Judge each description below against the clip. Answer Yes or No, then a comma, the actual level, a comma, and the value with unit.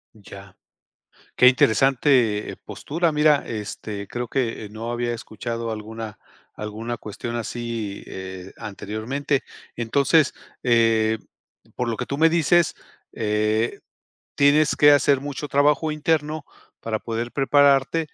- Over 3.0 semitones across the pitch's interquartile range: Yes, average, 4.6 semitones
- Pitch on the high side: No, low, 120 Hz